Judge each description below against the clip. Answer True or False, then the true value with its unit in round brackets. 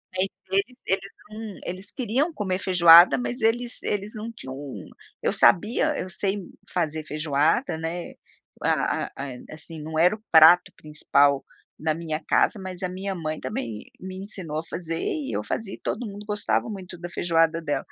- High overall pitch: False (180 Hz)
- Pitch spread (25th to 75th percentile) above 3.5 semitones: True (4.5 semitones)